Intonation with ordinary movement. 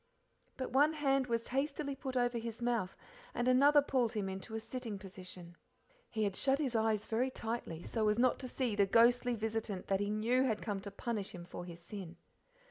Yes: average, 4.0 semitones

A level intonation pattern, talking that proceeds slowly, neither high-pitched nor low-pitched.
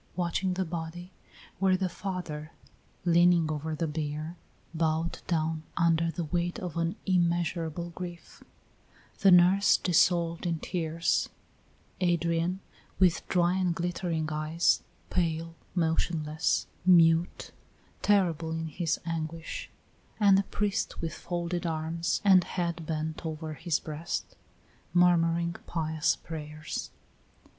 Yes: narrow, 1.7 semitones; slow, 115 wpm; medium, 170 Hz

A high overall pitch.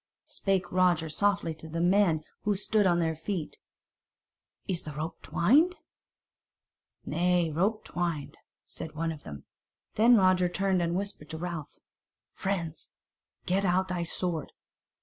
No: medium, 175 Hz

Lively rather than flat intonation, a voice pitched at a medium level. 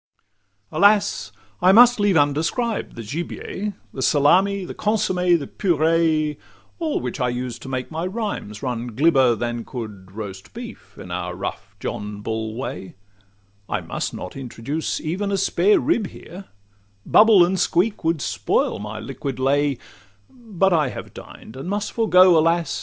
Yes: wide, 7.5 semitones; medium, 160 Hz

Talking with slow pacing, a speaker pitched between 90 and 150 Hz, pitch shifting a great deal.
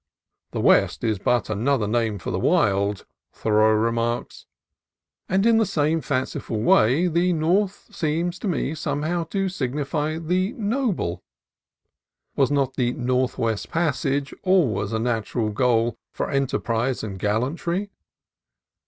Yes: slow, 125 wpm; low, 135 Hz; wide, 7.0 semitones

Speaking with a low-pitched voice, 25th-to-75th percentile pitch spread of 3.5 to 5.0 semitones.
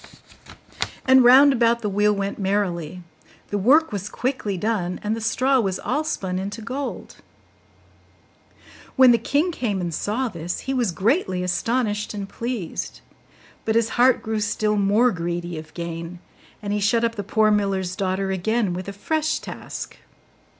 No: high, 210 Hz; average, 4.2 semitones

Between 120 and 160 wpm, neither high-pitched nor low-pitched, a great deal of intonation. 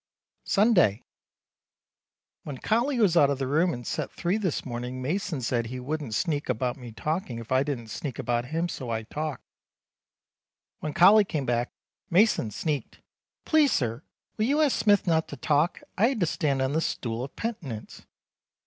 No: average, 175 wpm; medium, 145 Hz; wide, 6.6 semitones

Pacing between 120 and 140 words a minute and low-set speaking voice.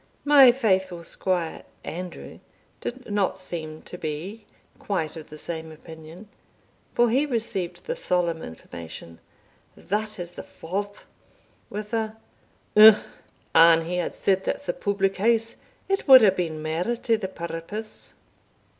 No: slow, 135 wpm; high, 190 Hz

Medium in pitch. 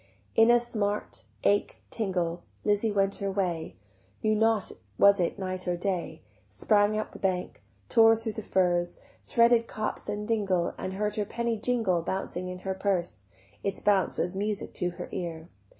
No: high, 200 Hz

